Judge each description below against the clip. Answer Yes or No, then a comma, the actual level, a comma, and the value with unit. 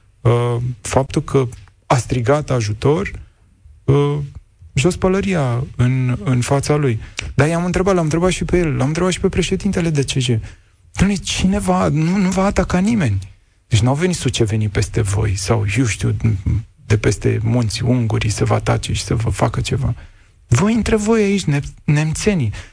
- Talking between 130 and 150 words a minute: No, average, 160 wpm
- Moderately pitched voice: No, low, 125 Hz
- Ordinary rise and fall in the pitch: No, wide, 7.2 semitones